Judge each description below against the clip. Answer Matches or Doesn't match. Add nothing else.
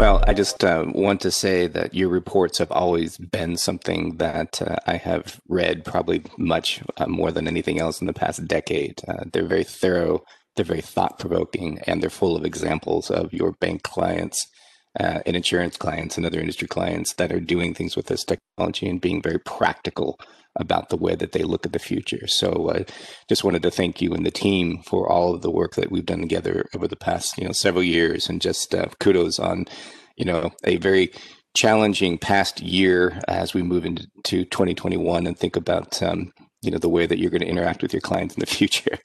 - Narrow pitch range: Matches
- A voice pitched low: Matches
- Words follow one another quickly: Matches